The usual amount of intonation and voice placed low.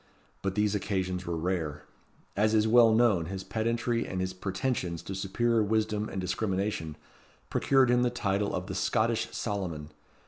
Yes: average, 3.2 semitones; low, 100 Hz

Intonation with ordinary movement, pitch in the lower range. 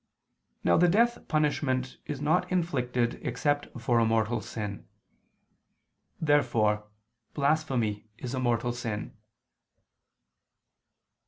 Yes: average, 4.6 semitones; low, 125 Hz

